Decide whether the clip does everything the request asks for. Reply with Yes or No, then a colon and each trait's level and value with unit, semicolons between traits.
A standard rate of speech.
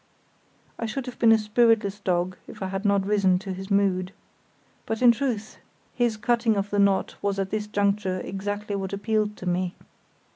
Yes: average, 185 wpm